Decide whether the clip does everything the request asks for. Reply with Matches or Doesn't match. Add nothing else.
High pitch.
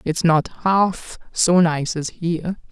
Doesn't match